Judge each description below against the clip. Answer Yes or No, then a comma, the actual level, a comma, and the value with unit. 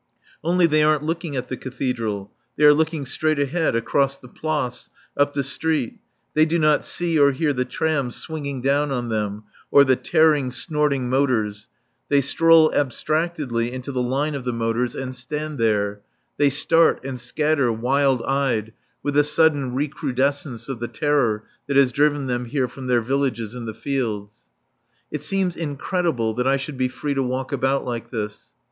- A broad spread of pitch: No, average, 3.4 semitones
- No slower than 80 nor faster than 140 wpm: No, average, 175 wpm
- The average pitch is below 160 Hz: Yes, low, 135 Hz